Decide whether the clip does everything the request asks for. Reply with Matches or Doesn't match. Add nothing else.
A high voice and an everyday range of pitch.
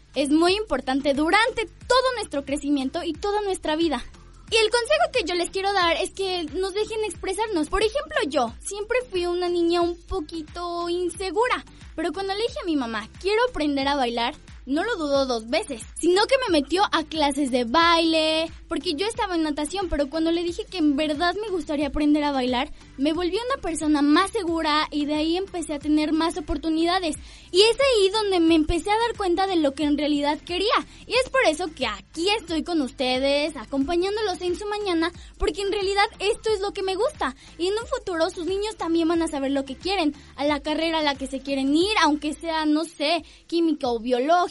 Matches